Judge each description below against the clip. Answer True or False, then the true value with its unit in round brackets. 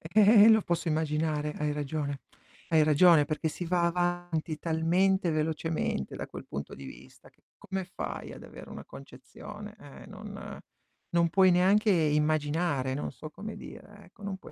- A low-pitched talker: False (165 Hz)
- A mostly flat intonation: False (3.2 semitones)